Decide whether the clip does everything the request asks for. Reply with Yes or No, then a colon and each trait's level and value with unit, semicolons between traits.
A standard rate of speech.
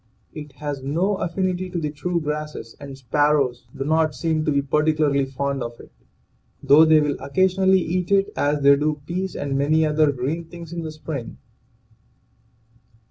Yes: average, 170 wpm